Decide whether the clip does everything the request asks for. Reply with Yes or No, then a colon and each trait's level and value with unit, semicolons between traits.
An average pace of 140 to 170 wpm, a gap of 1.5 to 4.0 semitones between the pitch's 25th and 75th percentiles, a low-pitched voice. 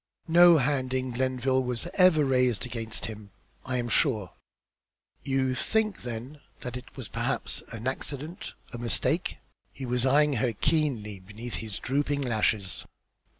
Yes: average, 150 wpm; average, 3.3 semitones; low, 130 Hz